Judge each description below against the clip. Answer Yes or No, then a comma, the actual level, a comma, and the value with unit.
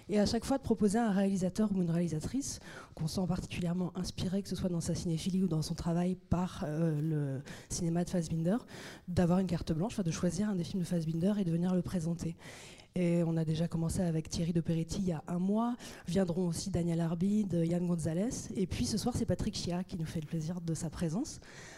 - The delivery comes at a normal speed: No, fast, 230 wpm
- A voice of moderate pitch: Yes, medium, 175 Hz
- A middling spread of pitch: No, narrow, 2.3 semitones